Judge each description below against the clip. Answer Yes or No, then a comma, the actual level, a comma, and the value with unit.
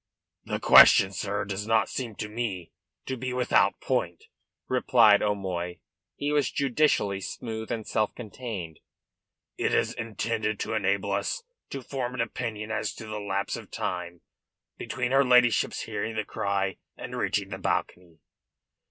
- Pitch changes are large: No, average, 3.6 semitones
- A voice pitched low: Yes, low, 110 Hz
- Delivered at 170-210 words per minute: No, average, 150 wpm